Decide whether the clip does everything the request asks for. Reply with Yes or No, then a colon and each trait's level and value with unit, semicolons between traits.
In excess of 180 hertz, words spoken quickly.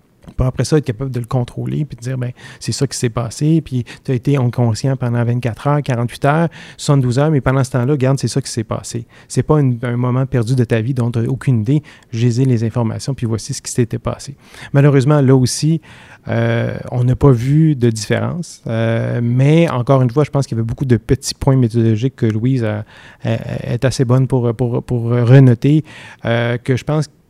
No: low, 130 Hz; fast, 230 wpm